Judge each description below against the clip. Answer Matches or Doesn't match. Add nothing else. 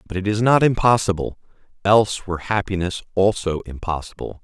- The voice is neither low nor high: Doesn't match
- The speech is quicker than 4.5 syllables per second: Matches